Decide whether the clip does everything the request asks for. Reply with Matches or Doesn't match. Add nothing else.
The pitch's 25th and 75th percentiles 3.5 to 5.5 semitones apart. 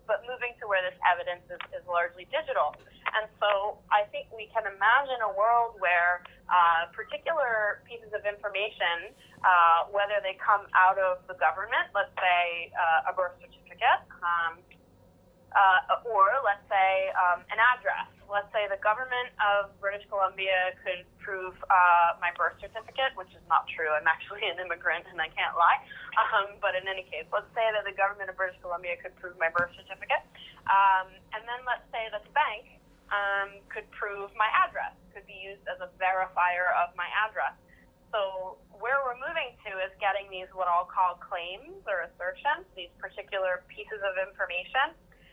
Doesn't match